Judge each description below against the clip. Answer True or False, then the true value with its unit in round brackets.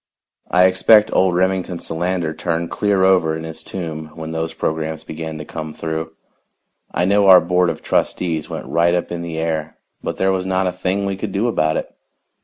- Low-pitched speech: True (85 Hz)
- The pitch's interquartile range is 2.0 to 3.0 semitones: True (2.6 semitones)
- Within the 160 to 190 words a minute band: False (200 wpm)